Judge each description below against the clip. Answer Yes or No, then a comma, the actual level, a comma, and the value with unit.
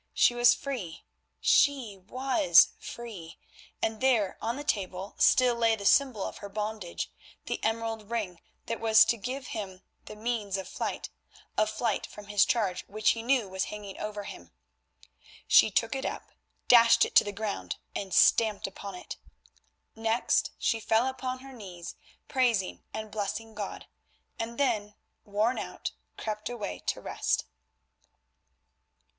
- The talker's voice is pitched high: Yes, high, 220 Hz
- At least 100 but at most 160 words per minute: Yes, average, 150 wpm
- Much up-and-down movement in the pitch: No, average, 2.9 semitones